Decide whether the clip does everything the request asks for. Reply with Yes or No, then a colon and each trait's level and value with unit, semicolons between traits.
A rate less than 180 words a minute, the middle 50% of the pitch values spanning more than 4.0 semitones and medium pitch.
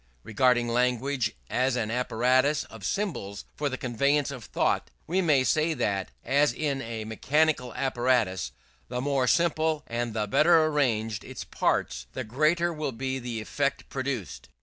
No: average, 150 wpm; average, 4.5 semitones; low, 130 Hz